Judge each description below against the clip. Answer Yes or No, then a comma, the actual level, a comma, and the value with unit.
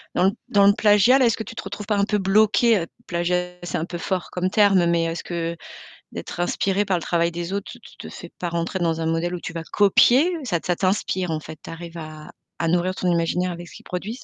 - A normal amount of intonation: Yes, average, 3.0 semitones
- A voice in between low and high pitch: Yes, medium, 180 Hz